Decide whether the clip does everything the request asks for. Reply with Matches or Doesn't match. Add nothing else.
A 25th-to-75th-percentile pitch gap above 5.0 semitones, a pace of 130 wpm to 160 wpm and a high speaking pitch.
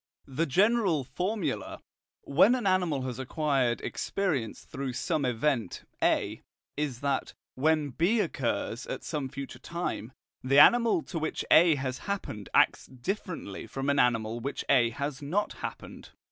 Doesn't match